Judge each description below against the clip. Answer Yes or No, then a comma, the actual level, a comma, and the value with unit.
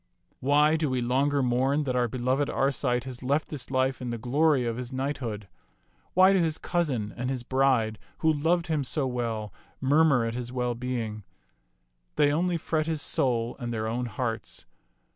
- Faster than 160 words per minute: Yes, average, 180 wpm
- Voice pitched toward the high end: No, low, 130 Hz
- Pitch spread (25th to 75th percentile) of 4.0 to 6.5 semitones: No, average, 3.4 semitones